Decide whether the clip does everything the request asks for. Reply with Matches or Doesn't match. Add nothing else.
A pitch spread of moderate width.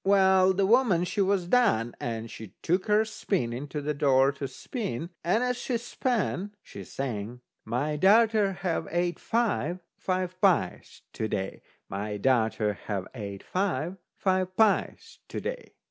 Doesn't match